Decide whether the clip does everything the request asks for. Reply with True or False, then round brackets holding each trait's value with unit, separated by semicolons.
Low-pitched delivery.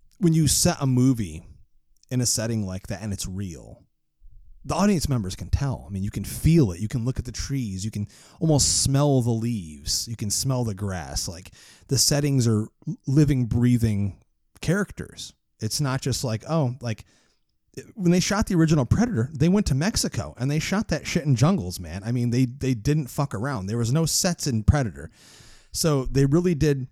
True (125 Hz)